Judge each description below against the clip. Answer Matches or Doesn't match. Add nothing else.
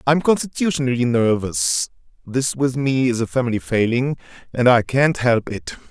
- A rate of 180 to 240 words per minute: Doesn't match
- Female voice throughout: Doesn't match